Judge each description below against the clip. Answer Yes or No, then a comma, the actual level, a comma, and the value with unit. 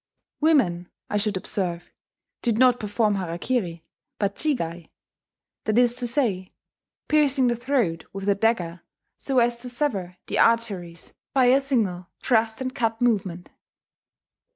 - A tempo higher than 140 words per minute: No, slow, 135 wpm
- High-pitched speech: Yes, high, 225 Hz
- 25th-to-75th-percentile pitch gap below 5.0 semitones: No, average, 5.3 semitones